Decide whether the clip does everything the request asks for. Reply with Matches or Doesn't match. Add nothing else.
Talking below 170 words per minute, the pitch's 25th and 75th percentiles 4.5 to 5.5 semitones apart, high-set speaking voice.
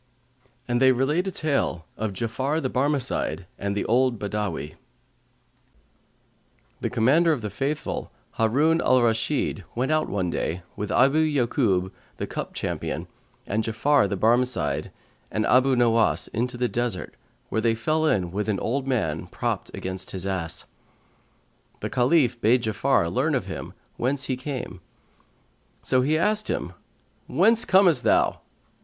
Doesn't match